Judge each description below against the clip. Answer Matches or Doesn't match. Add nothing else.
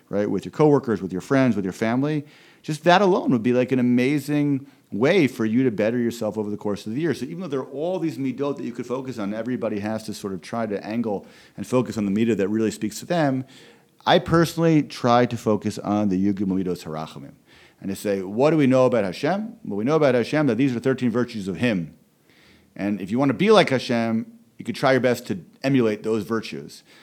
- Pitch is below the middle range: Matches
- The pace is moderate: Doesn't match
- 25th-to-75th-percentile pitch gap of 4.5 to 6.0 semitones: Matches